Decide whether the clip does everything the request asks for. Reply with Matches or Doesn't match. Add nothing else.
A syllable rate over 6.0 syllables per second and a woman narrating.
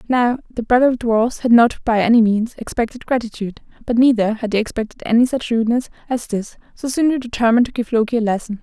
Matches